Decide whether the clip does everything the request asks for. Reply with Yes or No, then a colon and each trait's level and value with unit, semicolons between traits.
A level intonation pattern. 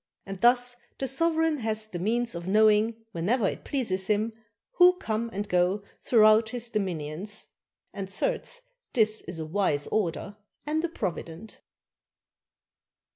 No: average, 4.3 semitones